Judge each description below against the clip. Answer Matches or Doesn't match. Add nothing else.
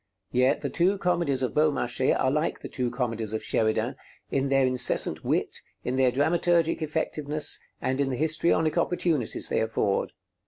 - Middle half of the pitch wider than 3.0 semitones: Matches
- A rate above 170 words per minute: Doesn't match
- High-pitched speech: Doesn't match